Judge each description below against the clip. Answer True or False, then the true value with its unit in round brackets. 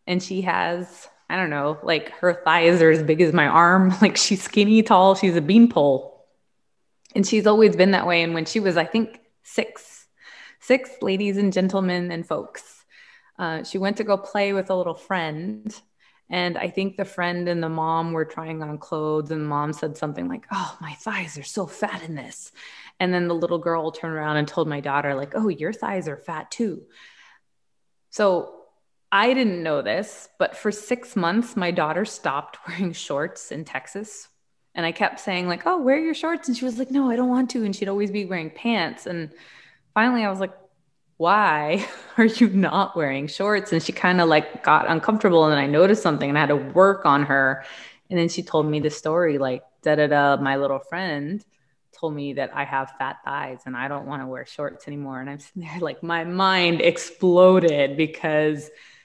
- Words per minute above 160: True (205 wpm)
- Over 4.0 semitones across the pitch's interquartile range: True (4.7 semitones)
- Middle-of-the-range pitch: True (175 Hz)